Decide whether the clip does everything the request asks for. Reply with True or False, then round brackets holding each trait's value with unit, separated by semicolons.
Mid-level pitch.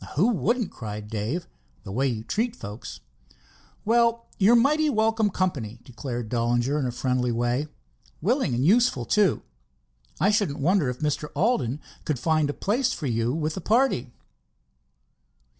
True (150 Hz)